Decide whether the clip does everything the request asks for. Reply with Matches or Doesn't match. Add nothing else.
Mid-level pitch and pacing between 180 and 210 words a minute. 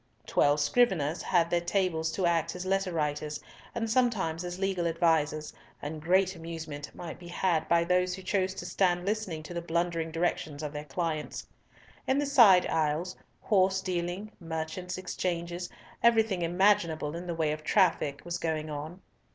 Doesn't match